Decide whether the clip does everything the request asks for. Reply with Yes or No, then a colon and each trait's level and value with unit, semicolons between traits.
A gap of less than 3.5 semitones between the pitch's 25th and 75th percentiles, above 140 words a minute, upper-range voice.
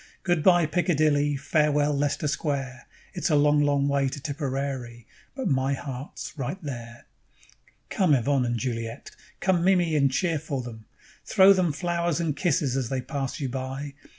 No: average, 3.1 semitones; average, 160 wpm; medium, 145 Hz